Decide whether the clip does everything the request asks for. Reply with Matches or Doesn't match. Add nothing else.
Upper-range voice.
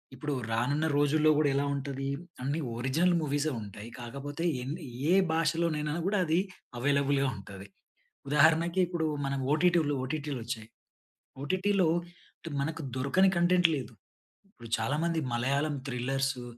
Doesn't match